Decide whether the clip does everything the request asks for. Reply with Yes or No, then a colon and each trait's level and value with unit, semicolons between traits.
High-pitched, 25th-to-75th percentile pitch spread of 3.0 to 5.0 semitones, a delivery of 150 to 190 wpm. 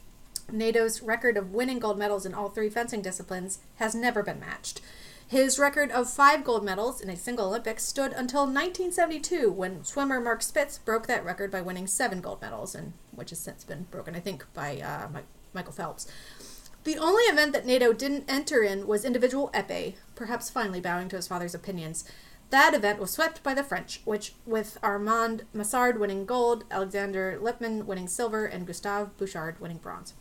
Yes: high, 225 Hz; average, 4.7 semitones; average, 185 wpm